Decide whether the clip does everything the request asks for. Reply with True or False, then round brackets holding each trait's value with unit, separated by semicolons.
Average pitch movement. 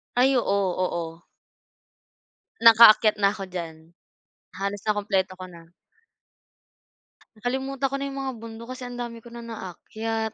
True (4.2 semitones)